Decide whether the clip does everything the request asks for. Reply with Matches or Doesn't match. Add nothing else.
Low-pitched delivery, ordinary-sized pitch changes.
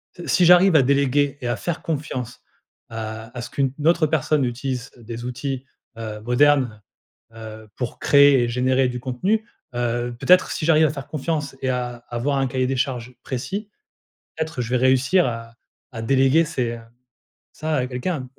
Matches